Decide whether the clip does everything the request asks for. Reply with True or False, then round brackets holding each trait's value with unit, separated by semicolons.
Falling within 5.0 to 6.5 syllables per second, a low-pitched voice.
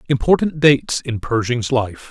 False (4.7 syllables/s; 130 Hz)